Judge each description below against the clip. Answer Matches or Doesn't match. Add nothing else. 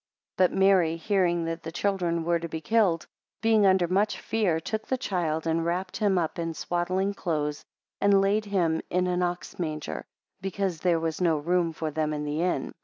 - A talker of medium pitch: Matches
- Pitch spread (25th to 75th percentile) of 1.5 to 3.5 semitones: Matches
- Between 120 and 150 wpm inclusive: Doesn't match